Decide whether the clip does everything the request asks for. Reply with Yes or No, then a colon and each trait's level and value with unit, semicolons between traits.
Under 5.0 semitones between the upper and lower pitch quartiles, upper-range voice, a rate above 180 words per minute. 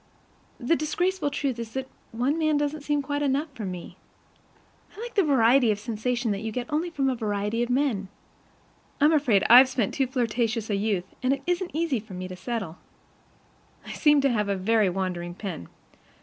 No: wide, 5.6 semitones; high, 245 Hz; average, 190 wpm